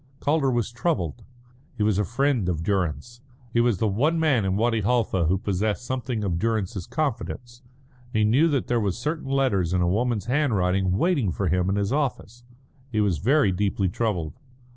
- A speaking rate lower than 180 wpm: No, average, 185 wpm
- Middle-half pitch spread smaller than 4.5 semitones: No, average, 4.8 semitones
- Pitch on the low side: Yes, low, 110 Hz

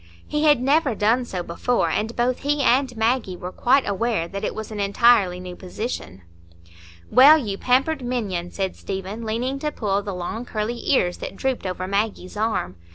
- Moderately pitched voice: No, high, 220 Hz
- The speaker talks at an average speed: Yes, average, 180 wpm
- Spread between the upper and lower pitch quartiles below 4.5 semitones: No, average, 4.8 semitones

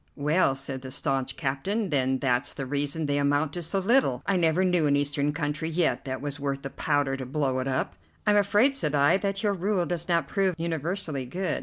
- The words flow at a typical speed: No, fast, 215 wpm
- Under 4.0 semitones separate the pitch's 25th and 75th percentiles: No, average, 4.8 semitones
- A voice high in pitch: No, medium, 150 Hz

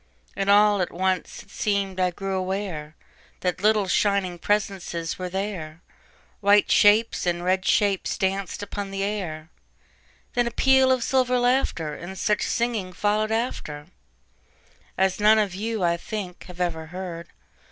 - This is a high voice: Yes, high, 195 Hz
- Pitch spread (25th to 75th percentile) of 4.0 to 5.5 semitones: No, average, 2.8 semitones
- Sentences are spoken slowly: Yes, slow, 130 wpm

